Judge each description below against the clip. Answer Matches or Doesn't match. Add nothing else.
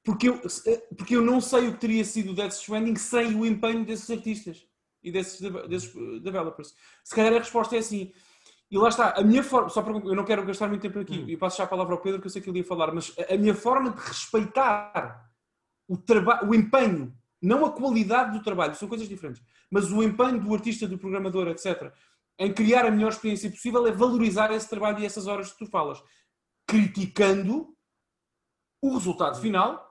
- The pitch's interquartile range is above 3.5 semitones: Doesn't match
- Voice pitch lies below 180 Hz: Doesn't match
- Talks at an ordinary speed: Doesn't match